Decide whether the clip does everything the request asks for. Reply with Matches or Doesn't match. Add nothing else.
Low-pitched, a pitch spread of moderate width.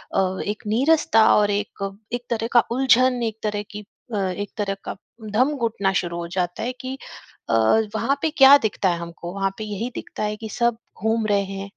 Doesn't match